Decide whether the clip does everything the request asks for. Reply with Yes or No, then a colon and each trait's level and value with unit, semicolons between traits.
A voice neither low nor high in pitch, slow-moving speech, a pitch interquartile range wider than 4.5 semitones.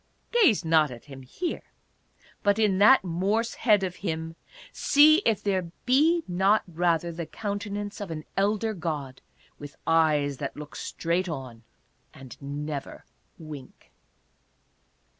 Yes: medium, 175 Hz; slow, 130 wpm; wide, 5.4 semitones